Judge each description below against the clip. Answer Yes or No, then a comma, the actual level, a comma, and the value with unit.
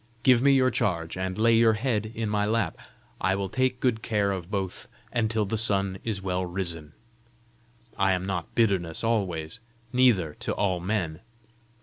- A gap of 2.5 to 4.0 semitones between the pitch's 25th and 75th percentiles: Yes, average, 3.7 semitones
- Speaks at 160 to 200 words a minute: Yes, average, 165 wpm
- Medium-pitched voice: No, low, 100 Hz